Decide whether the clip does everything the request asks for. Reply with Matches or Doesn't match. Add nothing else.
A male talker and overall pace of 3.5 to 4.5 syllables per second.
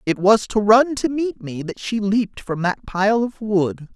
Matches